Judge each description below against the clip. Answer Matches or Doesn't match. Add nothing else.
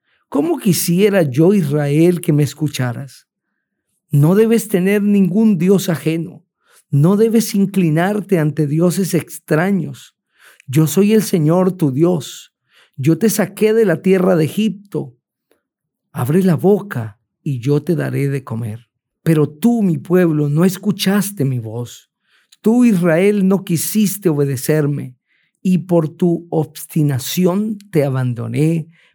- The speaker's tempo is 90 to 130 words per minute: Matches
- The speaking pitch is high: Doesn't match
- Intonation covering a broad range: Doesn't match